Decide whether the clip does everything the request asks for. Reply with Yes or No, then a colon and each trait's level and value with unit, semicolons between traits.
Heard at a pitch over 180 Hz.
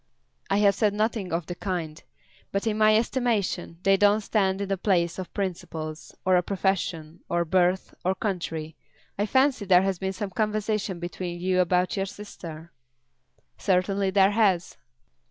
Yes: high, 190 Hz